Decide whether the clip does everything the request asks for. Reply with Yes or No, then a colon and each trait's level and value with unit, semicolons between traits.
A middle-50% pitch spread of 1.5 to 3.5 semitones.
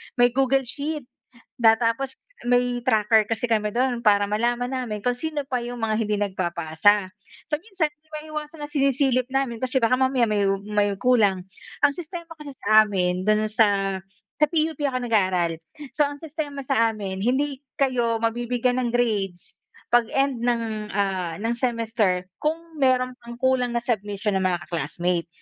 No: average, 4.3 semitones